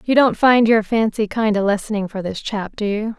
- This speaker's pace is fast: Yes, fast, 245 wpm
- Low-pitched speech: No, high, 215 Hz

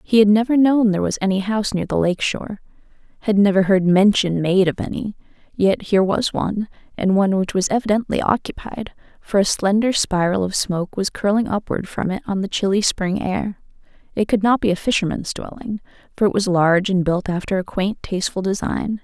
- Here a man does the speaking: No, female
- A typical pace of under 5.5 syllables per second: No, 5.7 syllables/s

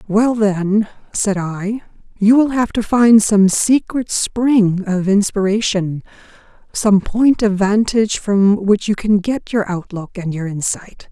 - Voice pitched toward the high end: Yes, high, 205 Hz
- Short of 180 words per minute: Yes, average, 150 wpm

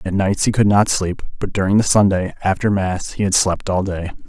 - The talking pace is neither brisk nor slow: No, fast, 240 wpm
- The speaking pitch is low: Yes, very low, 95 Hz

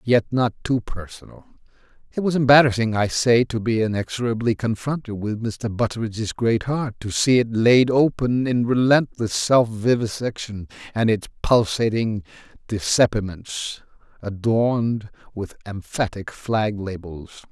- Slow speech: Yes, slow, 125 wpm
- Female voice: No, male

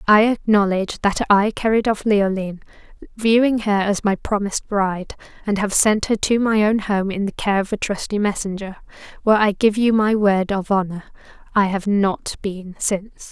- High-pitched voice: Yes, high, 205 Hz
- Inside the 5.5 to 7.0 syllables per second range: No, 5.1 syllables/s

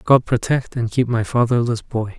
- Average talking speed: Yes, average, 190 wpm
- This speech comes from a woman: No, male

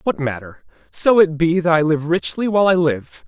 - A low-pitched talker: No, medium, 165 Hz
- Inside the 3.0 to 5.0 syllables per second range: No, 5.2 syllables/s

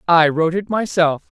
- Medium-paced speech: Yes, average, 170 wpm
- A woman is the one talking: Yes, female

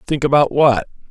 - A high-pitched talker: No, low, 135 Hz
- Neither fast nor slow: Yes, average, 165 wpm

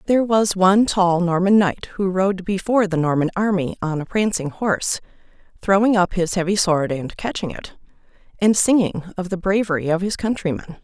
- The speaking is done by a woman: Yes, female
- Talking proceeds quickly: No, average, 175 wpm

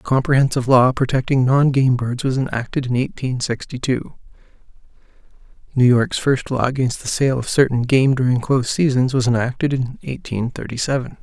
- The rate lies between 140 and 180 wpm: Yes, average, 170 wpm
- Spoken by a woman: No, male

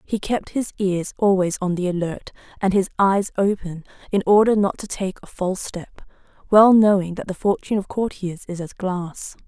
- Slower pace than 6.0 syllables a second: Yes, 5.0 syllables/s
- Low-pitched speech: No, high, 190 Hz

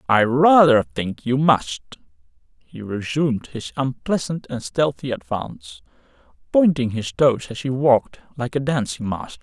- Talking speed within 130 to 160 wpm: Yes, average, 140 wpm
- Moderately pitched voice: No, low, 125 Hz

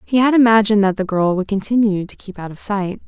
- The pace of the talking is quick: Yes, fast, 255 wpm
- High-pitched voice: Yes, high, 205 Hz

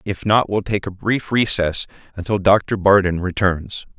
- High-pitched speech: No, low, 100 Hz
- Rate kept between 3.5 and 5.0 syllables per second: Yes, 4.6 syllables/s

